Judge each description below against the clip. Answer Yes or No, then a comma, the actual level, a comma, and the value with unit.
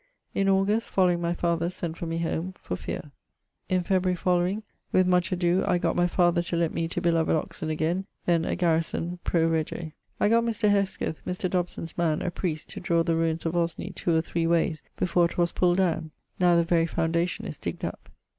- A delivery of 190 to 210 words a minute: Yes, fast, 205 wpm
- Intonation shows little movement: Yes, narrow, 1.7 semitones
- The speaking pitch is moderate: Yes, medium, 175 Hz